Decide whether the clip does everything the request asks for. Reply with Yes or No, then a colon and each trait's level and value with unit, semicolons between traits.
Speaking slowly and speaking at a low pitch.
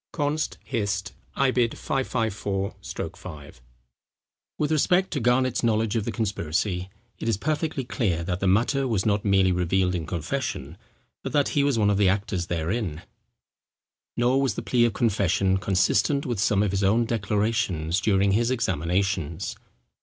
No: average, 155 wpm; low, 105 Hz